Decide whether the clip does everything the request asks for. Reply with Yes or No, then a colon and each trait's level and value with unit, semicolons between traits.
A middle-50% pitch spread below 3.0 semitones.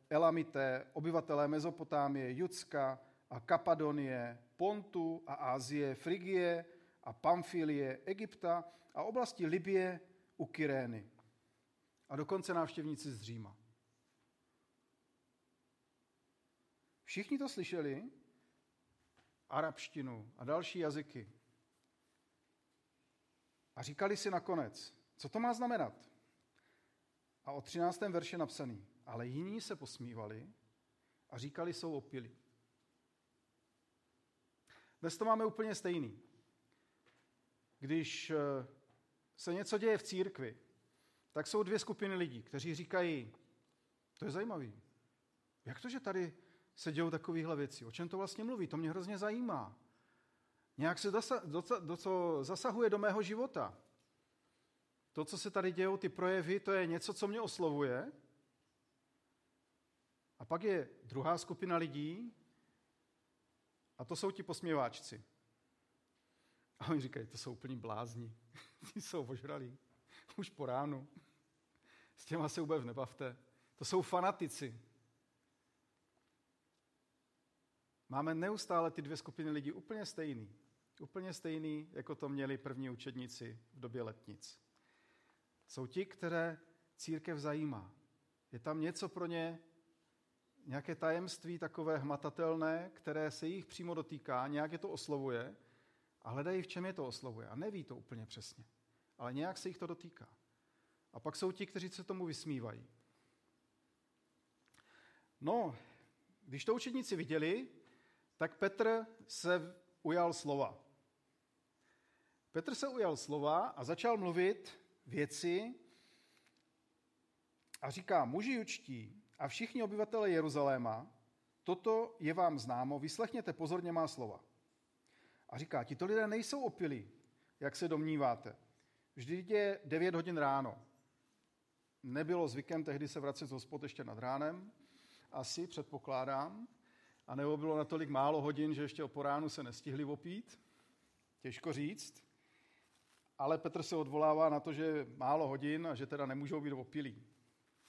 No: average, 4.9 semitones